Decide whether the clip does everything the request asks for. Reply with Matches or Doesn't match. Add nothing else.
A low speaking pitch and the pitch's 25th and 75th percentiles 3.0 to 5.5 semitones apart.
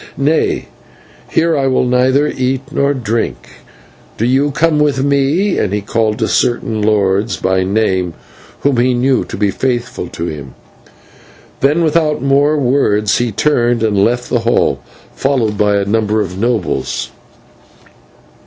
Matches